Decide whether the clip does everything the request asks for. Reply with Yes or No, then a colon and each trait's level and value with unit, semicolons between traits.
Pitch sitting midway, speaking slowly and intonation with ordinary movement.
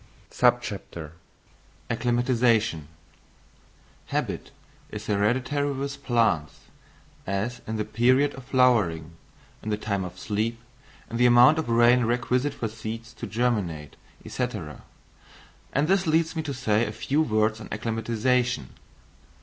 No: low, 115 Hz; slow, 120 wpm; average, 3.0 semitones